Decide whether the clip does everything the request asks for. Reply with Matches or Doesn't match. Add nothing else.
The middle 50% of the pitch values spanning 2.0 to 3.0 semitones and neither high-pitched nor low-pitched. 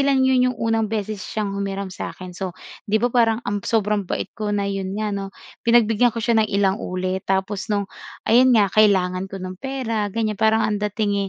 Doesn't match